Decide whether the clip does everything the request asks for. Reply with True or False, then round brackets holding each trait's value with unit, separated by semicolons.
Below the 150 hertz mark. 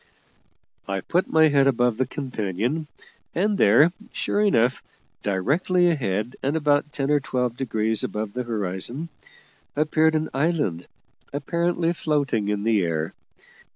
True (135 Hz)